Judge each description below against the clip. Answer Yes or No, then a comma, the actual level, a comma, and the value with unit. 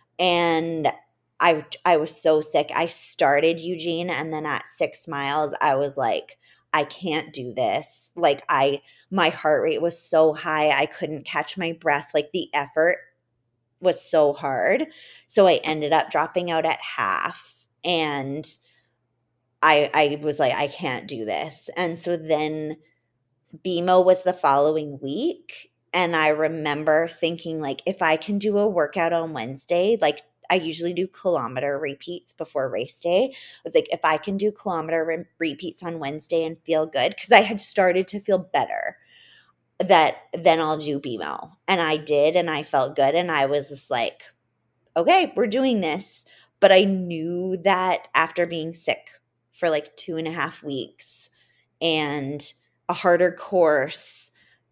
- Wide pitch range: No, average, 3.1 semitones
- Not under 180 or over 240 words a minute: No, average, 160 wpm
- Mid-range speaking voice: Yes, medium, 160 Hz